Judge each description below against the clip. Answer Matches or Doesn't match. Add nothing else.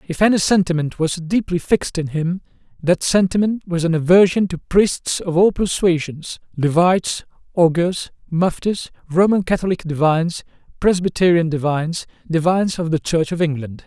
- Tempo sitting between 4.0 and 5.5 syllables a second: Matches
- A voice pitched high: Doesn't match